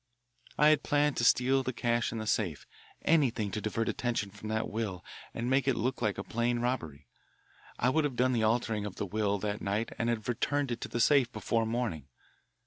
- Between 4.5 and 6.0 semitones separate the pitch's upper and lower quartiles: No, average, 3.1 semitones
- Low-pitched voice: Yes, low, 115 Hz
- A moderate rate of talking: No, fast, 215 wpm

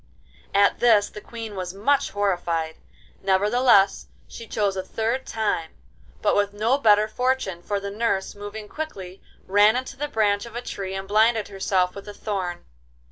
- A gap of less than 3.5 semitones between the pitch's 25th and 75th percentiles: Yes, average, 2.7 semitones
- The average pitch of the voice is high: Yes, high, 205 Hz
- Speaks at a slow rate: No, average, 165 wpm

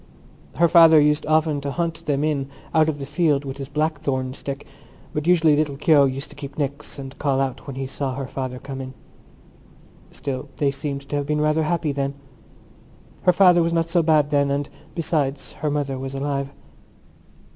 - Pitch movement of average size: No, narrow, 2.2 semitones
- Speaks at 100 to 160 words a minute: No, average, 190 wpm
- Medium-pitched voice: Yes, medium, 145 Hz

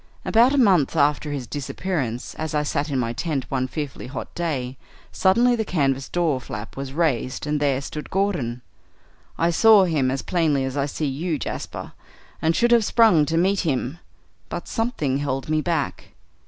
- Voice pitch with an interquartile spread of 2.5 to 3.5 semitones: No, average, 4.6 semitones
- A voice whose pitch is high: No, medium, 150 Hz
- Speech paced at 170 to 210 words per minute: Yes, average, 180 wpm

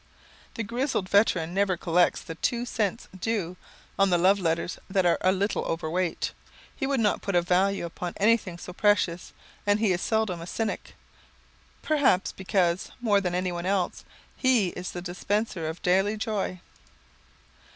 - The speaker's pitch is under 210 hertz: Yes, high, 190 Hz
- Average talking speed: Yes, average, 160 wpm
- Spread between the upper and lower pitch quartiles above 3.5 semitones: No, average, 3.1 semitones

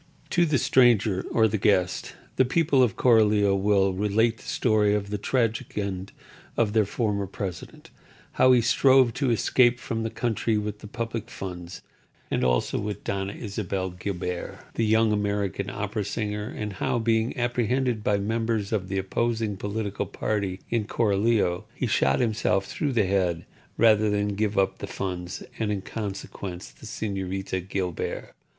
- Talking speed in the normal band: Yes, average, 160 wpm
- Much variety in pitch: No, average, 2.7 semitones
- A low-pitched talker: Yes, low, 105 Hz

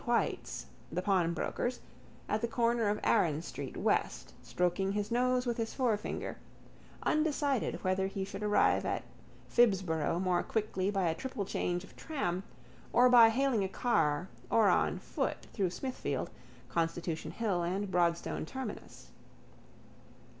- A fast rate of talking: No, slow, 135 wpm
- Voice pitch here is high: Yes, high, 200 Hz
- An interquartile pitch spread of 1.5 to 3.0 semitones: No, average, 5.1 semitones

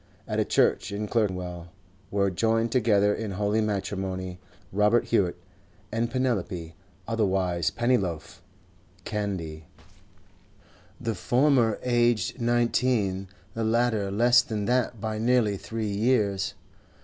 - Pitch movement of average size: Yes, average, 3.3 semitones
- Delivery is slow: Yes, slow, 110 wpm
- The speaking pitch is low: Yes, low, 105 Hz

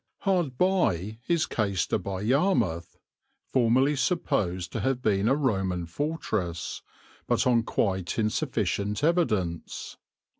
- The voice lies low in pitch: Yes, low, 110 Hz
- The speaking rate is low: Yes, slow, 110 wpm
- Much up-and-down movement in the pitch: Yes, wide, 7.2 semitones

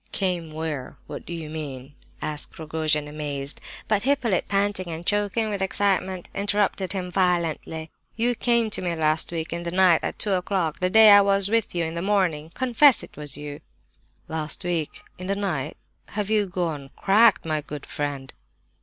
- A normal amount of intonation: Yes, average, 4.6 semitones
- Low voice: No, medium, 175 Hz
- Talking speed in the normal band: Yes, average, 180 wpm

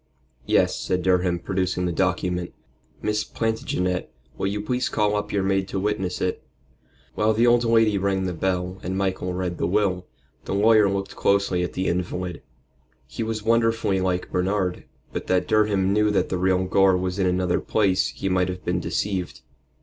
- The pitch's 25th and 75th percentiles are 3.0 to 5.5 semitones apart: No, narrow, 2.4 semitones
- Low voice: Yes, very low, 95 Hz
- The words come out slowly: No, average, 180 wpm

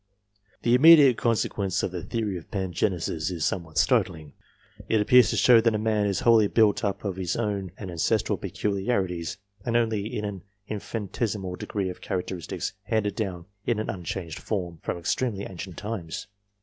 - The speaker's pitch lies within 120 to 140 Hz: No, low, 100 Hz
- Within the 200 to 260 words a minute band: No, average, 165 wpm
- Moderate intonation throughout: Yes, average, 3.5 semitones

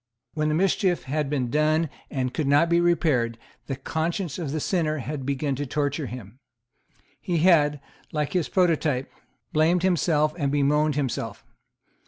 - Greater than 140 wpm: Yes, average, 155 wpm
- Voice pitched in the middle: Yes, medium, 150 Hz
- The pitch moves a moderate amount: Yes, average, 3.0 semitones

